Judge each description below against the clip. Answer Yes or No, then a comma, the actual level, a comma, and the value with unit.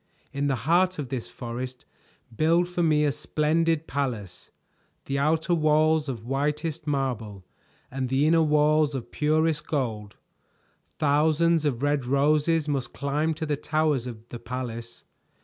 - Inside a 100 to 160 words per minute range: Yes, average, 145 wpm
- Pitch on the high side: No, medium, 145 Hz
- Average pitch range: Yes, average, 3.4 semitones